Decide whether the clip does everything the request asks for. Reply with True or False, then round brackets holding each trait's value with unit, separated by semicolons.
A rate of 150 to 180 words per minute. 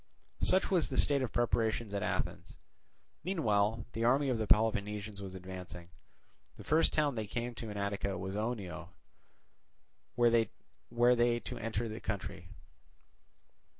False (140 wpm)